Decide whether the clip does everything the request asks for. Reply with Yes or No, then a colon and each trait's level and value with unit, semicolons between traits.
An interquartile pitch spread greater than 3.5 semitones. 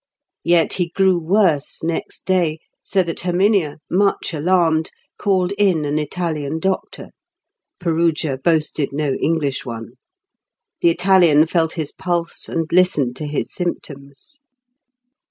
No: average, 3.2 semitones